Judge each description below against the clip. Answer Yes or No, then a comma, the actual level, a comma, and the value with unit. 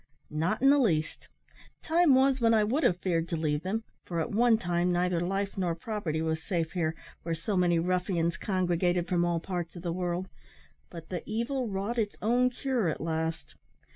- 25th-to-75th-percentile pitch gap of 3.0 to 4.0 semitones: No, average, 4.6 semitones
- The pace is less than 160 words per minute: No, average, 195 wpm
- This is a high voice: No, medium, 180 Hz